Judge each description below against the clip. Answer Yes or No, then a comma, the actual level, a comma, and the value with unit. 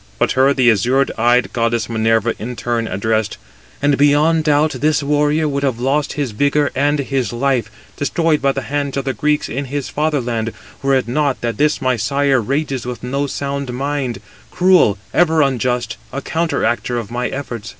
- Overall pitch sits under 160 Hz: Yes, low, 135 Hz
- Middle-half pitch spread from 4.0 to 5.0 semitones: No, average, 3.3 semitones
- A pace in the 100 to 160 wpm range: No, average, 180 wpm